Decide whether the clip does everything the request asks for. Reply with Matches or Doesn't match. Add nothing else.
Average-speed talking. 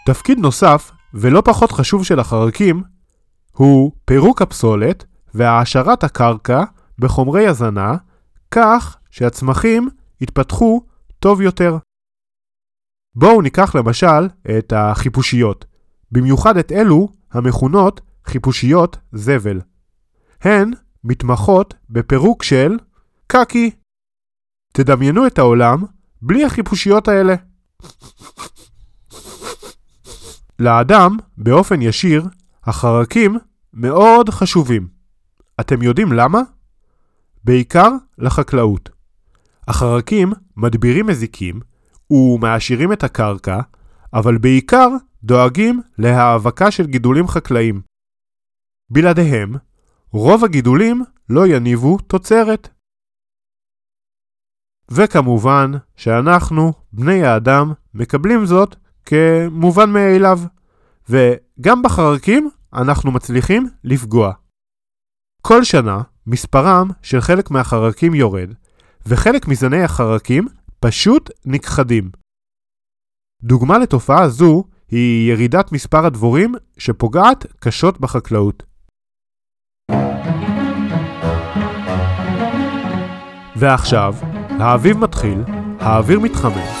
Doesn't match